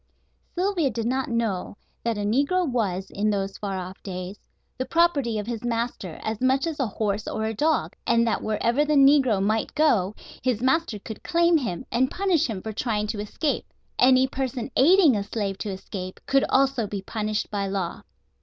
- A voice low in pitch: No, high, 230 Hz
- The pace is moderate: Yes, average, 190 wpm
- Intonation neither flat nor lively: Yes, average, 4.8 semitones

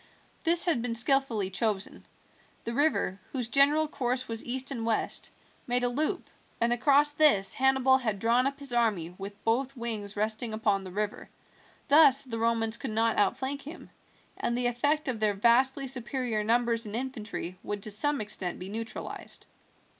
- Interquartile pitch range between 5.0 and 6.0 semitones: No, average, 3.7 semitones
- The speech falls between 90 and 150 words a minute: No, average, 170 wpm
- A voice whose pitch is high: Yes, high, 235 Hz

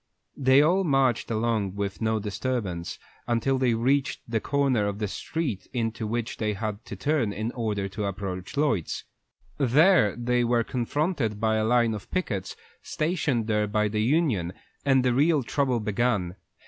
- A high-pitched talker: No, low, 115 Hz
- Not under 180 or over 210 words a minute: No, average, 160 wpm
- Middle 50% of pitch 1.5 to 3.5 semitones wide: No, average, 4.2 semitones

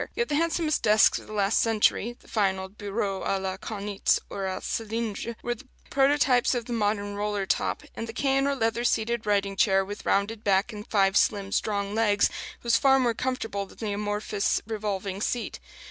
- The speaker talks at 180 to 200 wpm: Yes, average, 190 wpm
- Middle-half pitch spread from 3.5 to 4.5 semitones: No, average, 2.7 semitones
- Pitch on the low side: No, high, 210 Hz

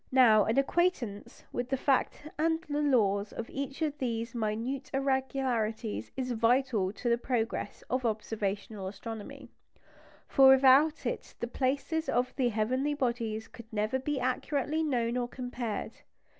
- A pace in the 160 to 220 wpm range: No, average, 145 wpm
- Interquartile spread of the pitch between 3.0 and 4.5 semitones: Yes, average, 3.4 semitones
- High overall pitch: Yes, very high, 250 Hz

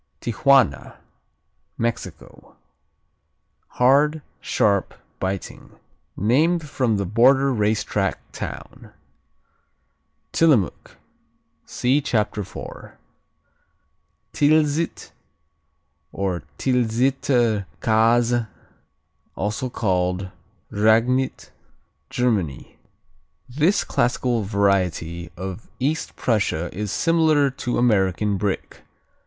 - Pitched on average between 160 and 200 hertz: No, low, 115 Hz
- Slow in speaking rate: Yes, slow, 70 wpm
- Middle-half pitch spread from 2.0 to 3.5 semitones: No, average, 5.1 semitones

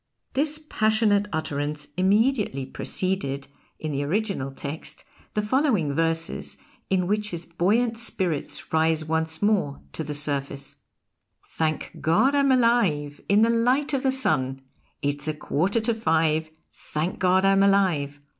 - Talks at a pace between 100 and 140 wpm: Yes, slow, 135 wpm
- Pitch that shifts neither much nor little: No, wide, 6.4 semitones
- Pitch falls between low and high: Yes, medium, 175 Hz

